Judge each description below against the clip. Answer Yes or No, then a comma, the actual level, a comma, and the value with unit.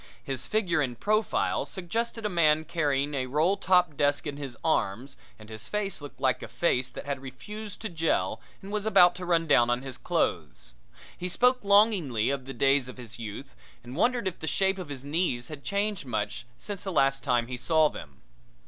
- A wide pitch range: Yes, wide, 6.6 semitones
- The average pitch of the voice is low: No, medium, 150 Hz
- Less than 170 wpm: No, average, 200 wpm